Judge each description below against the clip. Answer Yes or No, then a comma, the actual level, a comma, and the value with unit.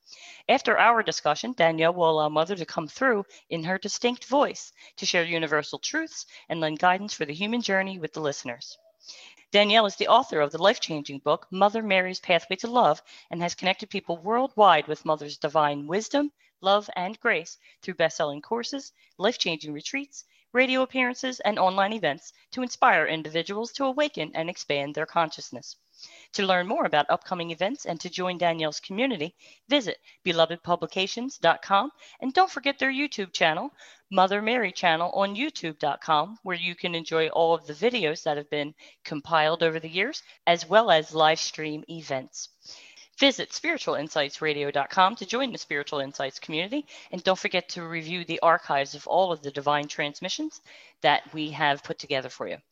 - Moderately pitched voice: Yes, medium, 180 Hz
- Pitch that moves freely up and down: Yes, wide, 6.5 semitones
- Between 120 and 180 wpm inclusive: Yes, average, 165 wpm